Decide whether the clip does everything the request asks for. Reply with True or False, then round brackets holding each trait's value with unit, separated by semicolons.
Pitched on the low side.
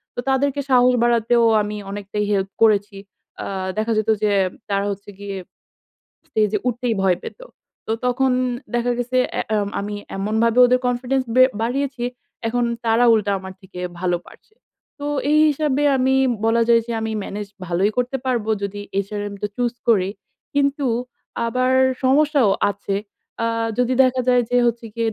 False (230 Hz)